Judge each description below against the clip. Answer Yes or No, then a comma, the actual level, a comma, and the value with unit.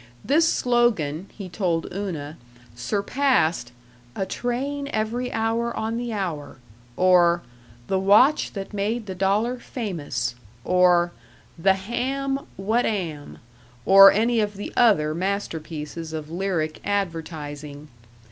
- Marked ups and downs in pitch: Yes, wide, 5.8 semitones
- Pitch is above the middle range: Yes, high, 195 Hz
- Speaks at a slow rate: Yes, slow, 115 wpm